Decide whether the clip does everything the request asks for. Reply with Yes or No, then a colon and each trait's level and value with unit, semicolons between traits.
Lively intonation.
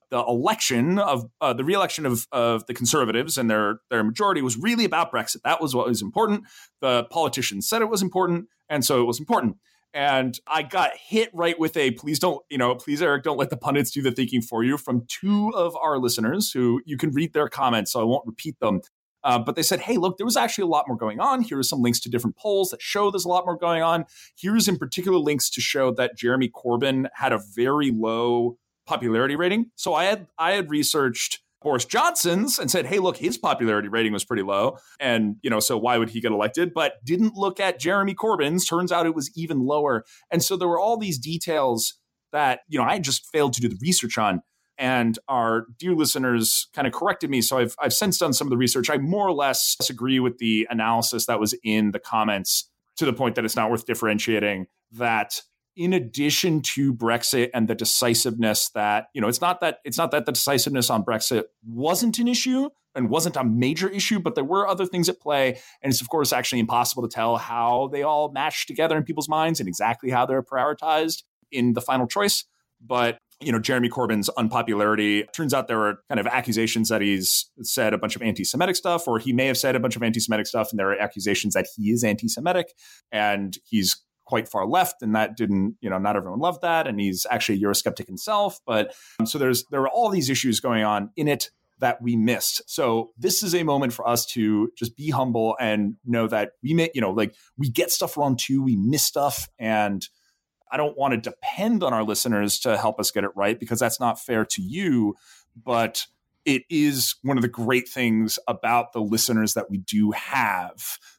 Yes: wide, 6.3 semitones